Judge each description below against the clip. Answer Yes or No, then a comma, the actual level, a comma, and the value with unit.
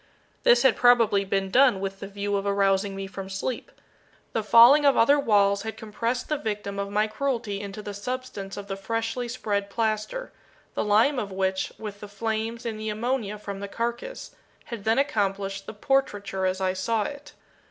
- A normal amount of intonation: Yes, average, 3.0 semitones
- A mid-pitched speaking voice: No, high, 210 Hz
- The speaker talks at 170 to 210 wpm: Yes, average, 185 wpm